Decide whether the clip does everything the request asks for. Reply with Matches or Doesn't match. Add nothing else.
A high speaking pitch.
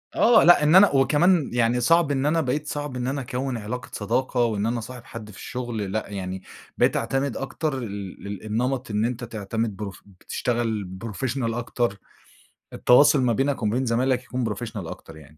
Doesn't match